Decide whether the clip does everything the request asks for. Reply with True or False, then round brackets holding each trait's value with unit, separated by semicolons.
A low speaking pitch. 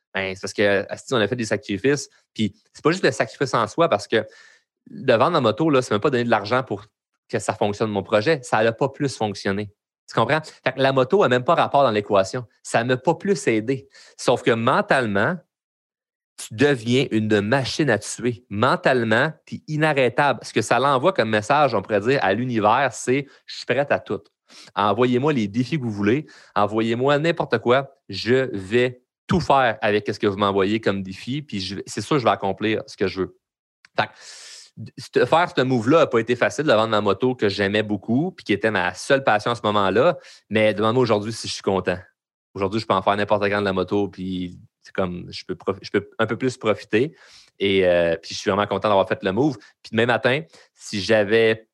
True (110 Hz)